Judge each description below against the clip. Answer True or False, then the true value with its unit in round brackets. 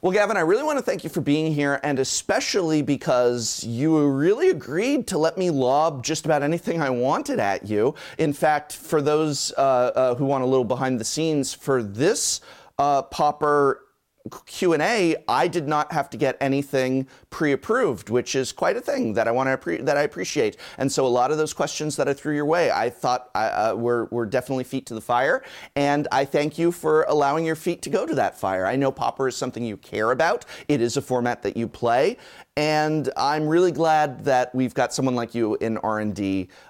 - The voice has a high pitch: False (140 Hz)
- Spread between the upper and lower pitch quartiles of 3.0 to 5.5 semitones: True (3.6 semitones)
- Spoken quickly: True (210 wpm)